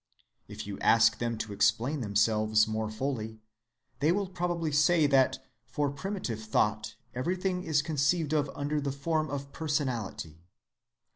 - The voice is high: No, medium, 140 Hz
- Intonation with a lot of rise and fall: Yes, wide, 6.1 semitones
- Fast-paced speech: No, average, 140 wpm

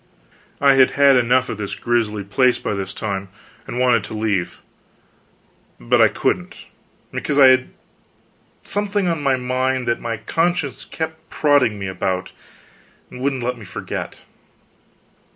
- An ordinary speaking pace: Yes, average, 145 wpm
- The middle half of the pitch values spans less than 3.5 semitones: No, average, 4.5 semitones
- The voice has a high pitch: No, low, 125 Hz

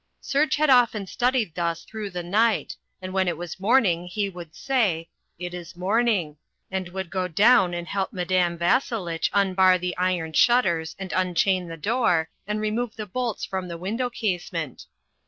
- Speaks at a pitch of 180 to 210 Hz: Yes, medium, 185 Hz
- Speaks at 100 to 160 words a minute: No, average, 170 wpm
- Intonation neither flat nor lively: Yes, average, 3.9 semitones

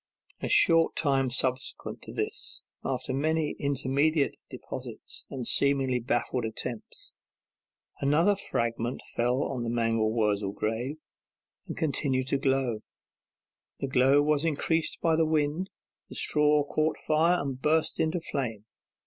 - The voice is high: No, medium, 140 Hz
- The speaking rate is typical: No, slow, 130 wpm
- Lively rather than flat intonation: No, average, 4.0 semitones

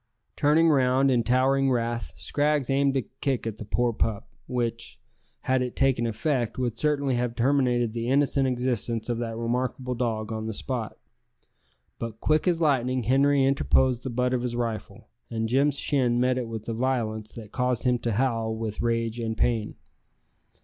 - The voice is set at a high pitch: No, low, 125 Hz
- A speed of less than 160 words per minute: No, average, 175 wpm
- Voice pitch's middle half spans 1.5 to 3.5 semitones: Yes, narrow, 2.5 semitones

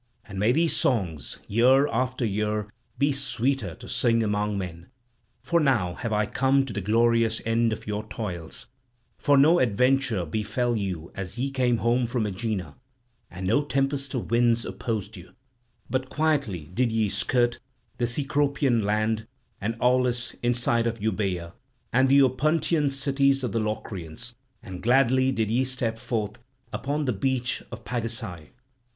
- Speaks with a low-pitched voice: Yes, low, 115 Hz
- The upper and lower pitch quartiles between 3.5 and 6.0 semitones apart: Yes, average, 3.8 semitones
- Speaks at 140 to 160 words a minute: Yes, average, 155 wpm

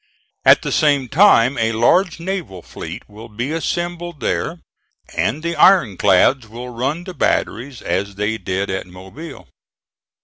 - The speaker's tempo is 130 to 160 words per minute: Yes, average, 145 wpm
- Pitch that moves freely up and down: Yes, wide, 8.2 semitones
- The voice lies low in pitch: Yes, low, 125 Hz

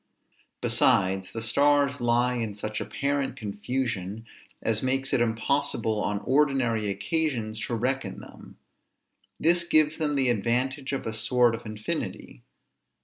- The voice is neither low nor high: No, low, 120 Hz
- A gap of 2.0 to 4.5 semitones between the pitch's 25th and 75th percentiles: Yes, average, 4.1 semitones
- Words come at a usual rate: No, slow, 130 wpm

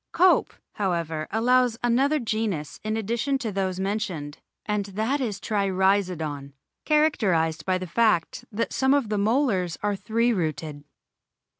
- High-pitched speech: Yes, high, 205 Hz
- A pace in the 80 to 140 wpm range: Yes, slow, 135 wpm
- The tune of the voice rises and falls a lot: No, average, 4.5 semitones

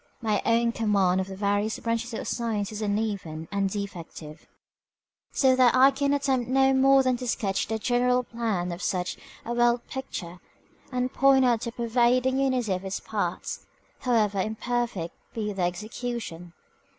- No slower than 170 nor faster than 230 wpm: No, average, 160 wpm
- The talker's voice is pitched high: Yes, high, 230 Hz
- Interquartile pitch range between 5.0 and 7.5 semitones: No, average, 4.0 semitones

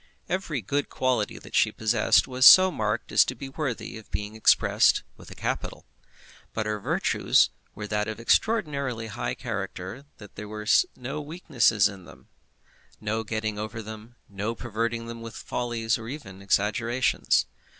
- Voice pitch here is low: Yes, low, 115 Hz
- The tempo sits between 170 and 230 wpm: No, average, 160 wpm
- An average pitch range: Yes, average, 3.2 semitones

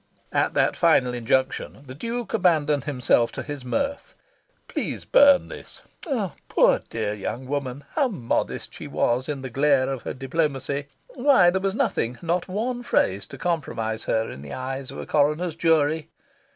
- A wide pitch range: Yes, wide, 5.7 semitones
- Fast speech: No, average, 165 wpm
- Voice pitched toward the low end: No, medium, 145 Hz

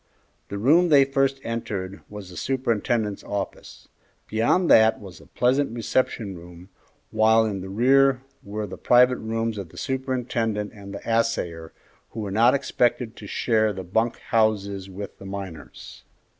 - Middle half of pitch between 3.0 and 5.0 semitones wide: Yes, average, 3.7 semitones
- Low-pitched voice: Yes, low, 110 Hz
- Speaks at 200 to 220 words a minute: No, average, 155 wpm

